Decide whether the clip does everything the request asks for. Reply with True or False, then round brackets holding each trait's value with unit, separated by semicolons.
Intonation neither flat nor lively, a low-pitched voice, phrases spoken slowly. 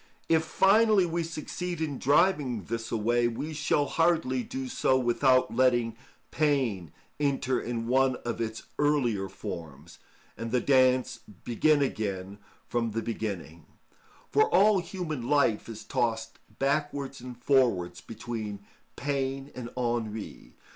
True (4.3 semitones; 125 Hz; 125 wpm)